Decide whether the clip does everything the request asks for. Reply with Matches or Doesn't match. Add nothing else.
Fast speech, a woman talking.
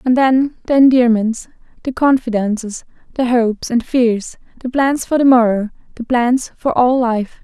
Doesn't match